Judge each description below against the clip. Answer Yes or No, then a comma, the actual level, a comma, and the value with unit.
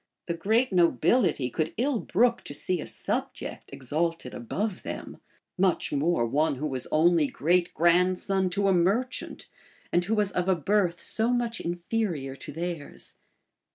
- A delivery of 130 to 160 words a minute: Yes, average, 155 wpm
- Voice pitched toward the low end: No, medium, 175 Hz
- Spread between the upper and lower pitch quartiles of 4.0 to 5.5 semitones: Yes, average, 4.4 semitones